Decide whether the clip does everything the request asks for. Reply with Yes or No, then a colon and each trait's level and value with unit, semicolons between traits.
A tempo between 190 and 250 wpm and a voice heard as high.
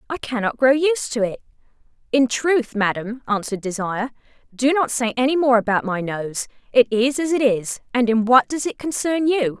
Yes: average, 195 wpm; high, 245 Hz